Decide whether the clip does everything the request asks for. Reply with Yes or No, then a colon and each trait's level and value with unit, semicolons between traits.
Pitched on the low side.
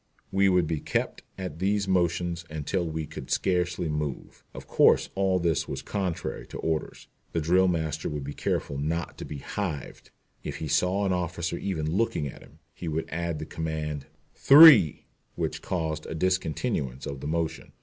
Yes: very low, 85 Hz